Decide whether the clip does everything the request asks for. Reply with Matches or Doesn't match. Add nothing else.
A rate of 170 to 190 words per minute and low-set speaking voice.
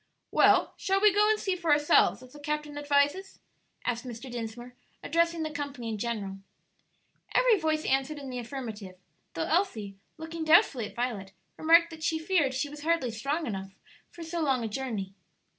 Doesn't match